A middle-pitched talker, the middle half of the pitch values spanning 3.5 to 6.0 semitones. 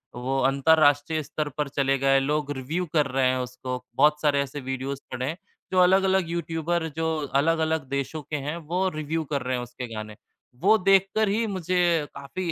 Yes: medium, 150 Hz; average, 3.9 semitones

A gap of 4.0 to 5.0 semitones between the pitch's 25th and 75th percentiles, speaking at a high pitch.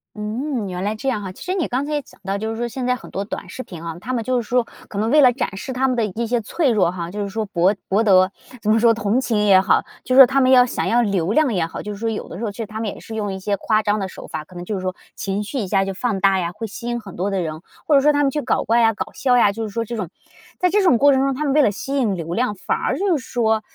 Yes: average, 4.4 semitones; high, 220 Hz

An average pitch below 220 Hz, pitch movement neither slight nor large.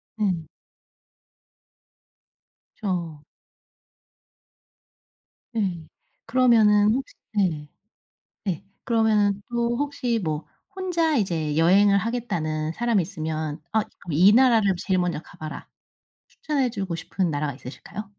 No: high, 200 Hz; wide, 6.0 semitones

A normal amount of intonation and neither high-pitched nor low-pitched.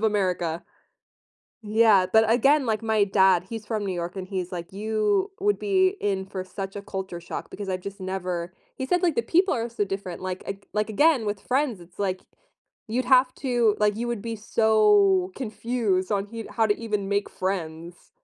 No: average, 3.5 semitones; high, 205 Hz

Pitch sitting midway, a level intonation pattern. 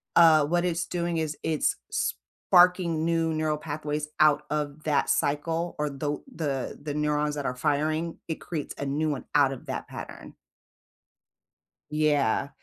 Yes: medium, 150 Hz; narrow, 1.9 semitones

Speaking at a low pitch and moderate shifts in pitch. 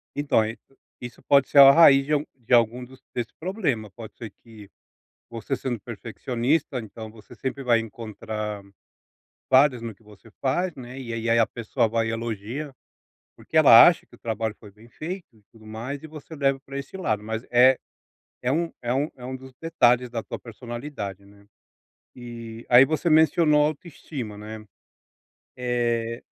Yes: low, 120 Hz; average, 3.6 semitones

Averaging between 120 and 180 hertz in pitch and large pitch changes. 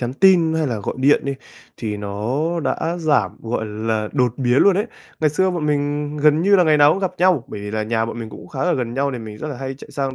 Yes: medium, 140 Hz; wide, 5.7 semitones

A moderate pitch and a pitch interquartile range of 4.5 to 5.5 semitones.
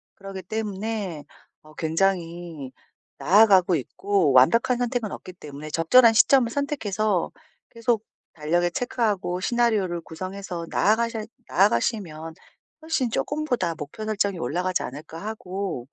No: high, 195 Hz; average, 5.1 semitones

